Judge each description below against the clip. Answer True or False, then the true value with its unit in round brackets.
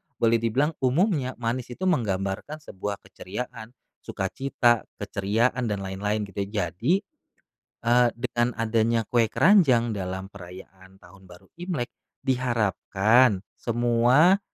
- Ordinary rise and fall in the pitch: True (4.0 semitones)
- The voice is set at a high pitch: False (115 Hz)